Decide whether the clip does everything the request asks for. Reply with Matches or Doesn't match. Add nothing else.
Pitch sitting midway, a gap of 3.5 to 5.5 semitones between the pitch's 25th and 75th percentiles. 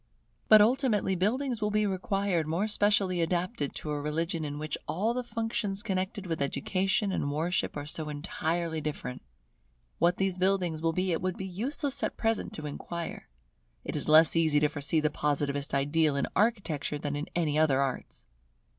Matches